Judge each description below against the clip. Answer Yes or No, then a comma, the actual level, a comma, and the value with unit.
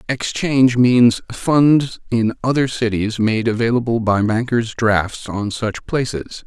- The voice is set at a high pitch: No, low, 115 Hz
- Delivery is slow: Yes, slow, 130 wpm